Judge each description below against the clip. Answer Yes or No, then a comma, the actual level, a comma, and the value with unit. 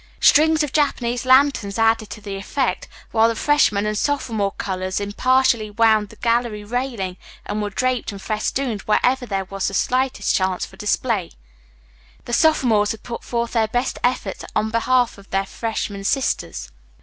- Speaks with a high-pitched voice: Yes, high, 225 Hz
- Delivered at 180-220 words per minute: No, average, 160 wpm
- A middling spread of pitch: Yes, average, 3.9 semitones